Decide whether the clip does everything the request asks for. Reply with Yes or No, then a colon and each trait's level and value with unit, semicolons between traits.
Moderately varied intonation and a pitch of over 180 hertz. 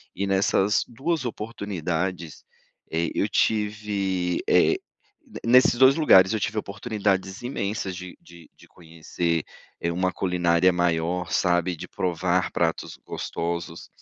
No: average, 3.4 semitones; very low, 95 Hz